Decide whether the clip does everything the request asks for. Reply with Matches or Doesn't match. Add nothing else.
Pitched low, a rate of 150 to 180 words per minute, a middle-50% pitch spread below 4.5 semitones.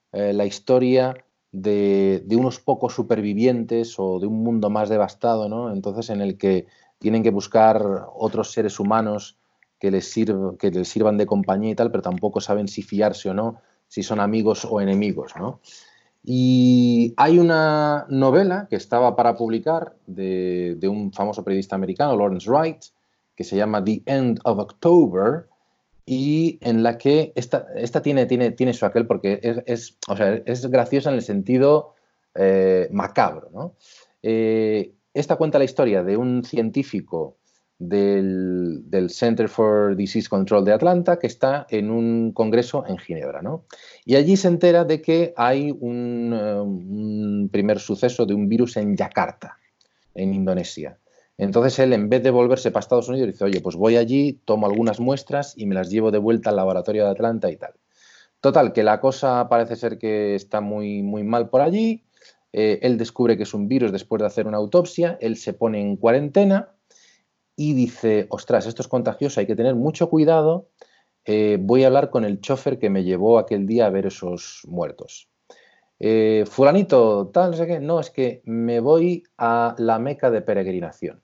Matches